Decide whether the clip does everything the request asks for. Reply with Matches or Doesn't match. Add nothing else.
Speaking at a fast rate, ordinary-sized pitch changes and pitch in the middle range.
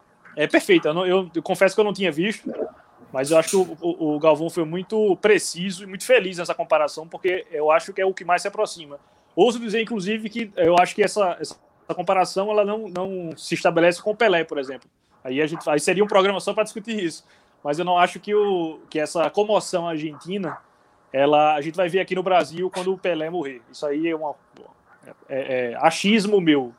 Matches